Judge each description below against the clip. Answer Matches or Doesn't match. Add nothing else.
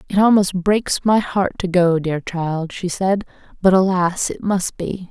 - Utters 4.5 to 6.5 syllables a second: Doesn't match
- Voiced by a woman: Matches